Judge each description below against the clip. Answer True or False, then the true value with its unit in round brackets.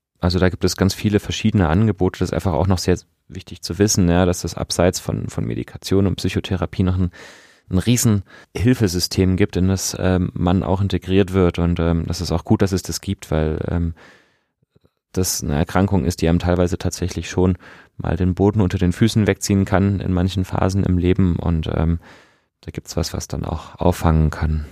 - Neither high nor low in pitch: False (90 Hz)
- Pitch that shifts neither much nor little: False (2.1 semitones)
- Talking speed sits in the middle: False (205 wpm)